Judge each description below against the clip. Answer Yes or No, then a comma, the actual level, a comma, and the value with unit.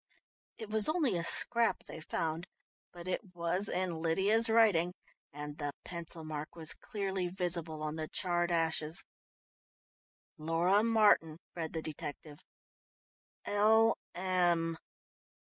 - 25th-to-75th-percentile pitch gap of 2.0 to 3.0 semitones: No, average, 3.8 semitones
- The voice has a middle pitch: Yes, medium, 175 Hz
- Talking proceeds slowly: Yes, slow, 115 wpm